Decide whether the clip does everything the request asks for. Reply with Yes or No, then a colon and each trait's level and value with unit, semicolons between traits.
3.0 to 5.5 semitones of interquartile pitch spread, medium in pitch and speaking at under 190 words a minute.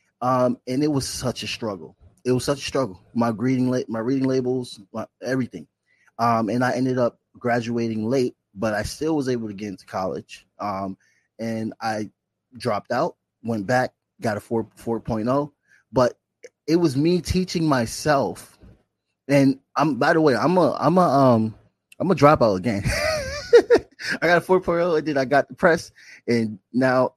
No: average, 3.8 semitones; low, 125 Hz; average, 175 wpm